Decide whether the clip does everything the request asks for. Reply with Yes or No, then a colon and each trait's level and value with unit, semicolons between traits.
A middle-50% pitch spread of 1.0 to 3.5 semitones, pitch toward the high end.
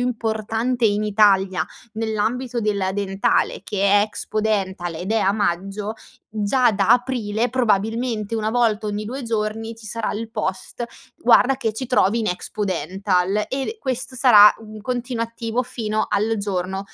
Yes: narrow, 2.5 semitones; high, 215 Hz